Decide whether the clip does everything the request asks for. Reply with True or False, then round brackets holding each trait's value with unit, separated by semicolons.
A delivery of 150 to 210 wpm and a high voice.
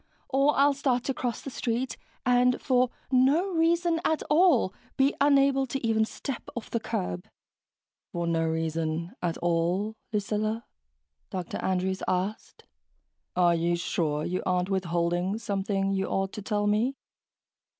False (140 wpm; 205 Hz)